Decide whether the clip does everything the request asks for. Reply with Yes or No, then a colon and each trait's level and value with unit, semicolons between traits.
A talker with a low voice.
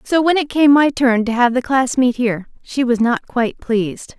No: very high, 250 Hz